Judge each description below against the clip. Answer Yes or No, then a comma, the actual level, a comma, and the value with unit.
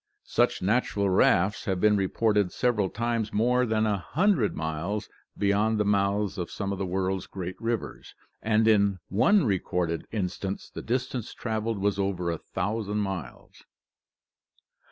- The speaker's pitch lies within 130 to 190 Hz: No, low, 105 Hz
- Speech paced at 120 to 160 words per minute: Yes, average, 145 wpm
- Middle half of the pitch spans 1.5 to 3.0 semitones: Yes, narrow, 2.6 semitones